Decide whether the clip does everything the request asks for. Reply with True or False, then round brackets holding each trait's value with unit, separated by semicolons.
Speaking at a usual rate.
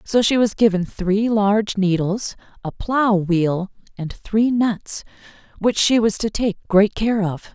True (165 wpm)